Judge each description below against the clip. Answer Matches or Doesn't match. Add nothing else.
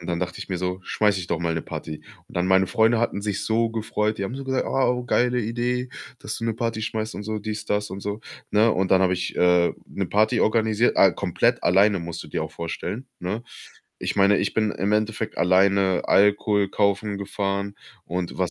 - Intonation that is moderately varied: Matches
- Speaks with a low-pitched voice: Matches